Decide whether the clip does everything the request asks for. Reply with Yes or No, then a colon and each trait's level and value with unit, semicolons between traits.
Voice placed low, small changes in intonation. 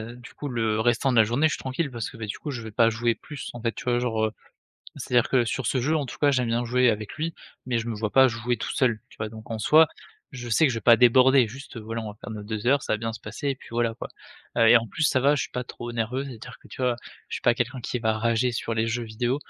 Yes: low, 120 Hz; narrow, 2.3 semitones